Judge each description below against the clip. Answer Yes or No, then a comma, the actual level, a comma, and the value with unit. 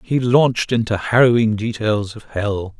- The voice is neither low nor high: No, low, 110 Hz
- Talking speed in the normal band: Yes, average, 150 wpm